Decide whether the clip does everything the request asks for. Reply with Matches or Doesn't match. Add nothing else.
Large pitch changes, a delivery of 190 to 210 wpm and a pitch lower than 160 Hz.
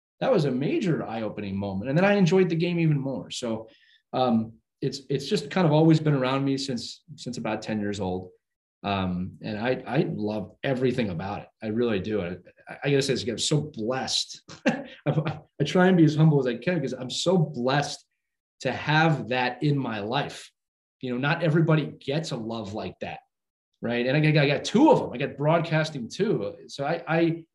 Matches